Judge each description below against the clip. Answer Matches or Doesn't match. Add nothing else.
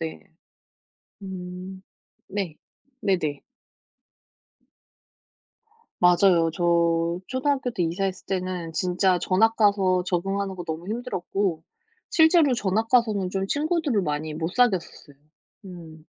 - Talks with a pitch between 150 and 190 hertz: Matches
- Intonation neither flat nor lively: Matches